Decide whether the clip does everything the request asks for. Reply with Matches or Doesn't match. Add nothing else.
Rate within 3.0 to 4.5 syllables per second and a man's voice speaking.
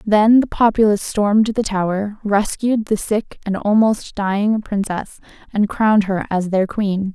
Doesn't match